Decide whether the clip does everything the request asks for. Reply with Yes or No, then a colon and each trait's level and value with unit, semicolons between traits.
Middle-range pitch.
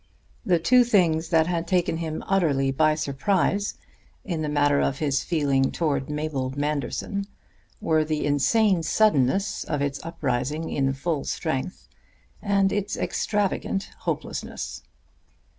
Yes: medium, 155 Hz